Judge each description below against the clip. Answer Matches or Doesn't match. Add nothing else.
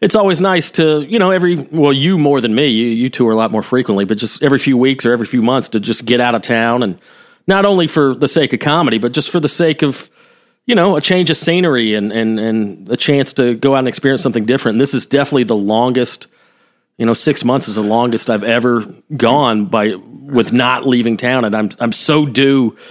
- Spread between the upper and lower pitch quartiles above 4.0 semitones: Matches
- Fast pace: Matches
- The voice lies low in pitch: Matches